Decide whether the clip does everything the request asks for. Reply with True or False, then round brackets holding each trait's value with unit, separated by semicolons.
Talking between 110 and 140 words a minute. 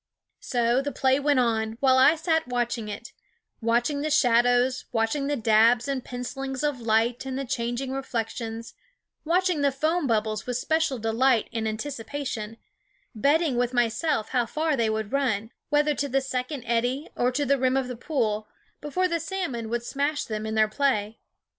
False (175 wpm)